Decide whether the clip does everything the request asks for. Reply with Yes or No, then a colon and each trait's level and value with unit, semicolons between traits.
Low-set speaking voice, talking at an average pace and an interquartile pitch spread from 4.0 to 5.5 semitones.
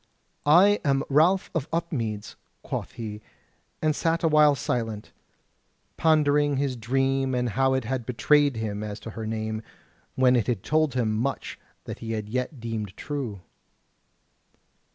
Yes: low, 130 Hz; average, 145 wpm; average, 4.7 semitones